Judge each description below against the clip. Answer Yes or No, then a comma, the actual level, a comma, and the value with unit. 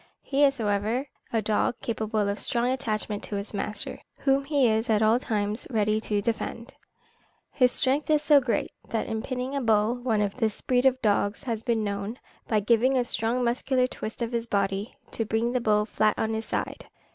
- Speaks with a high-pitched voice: Yes, high, 225 Hz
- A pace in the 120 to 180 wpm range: No, average, 200 wpm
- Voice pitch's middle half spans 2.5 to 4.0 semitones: Yes, average, 2.9 semitones